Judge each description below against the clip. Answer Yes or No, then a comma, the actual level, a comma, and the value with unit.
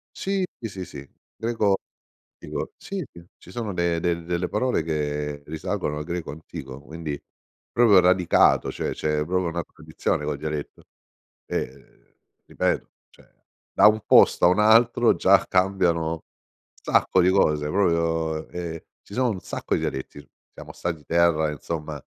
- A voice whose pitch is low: Yes, very low, 85 Hz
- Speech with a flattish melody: No, average, 3.7 semitones